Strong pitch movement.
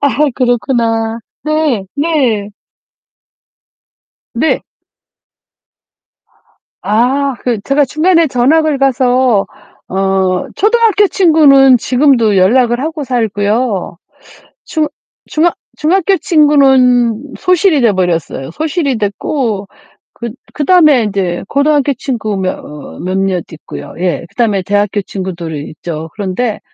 Yes: wide, 6.6 semitones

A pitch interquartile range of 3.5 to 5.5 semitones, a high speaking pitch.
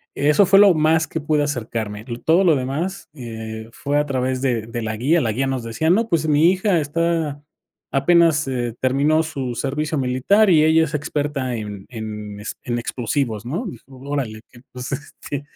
No: average, 4.8 semitones; medium, 140 Hz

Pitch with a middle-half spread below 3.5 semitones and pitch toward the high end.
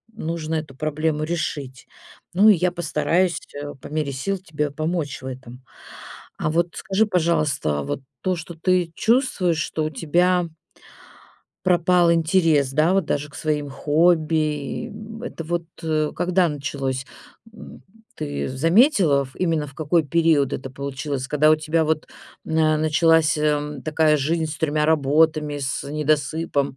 No: average, 2.7 semitones; medium, 155 Hz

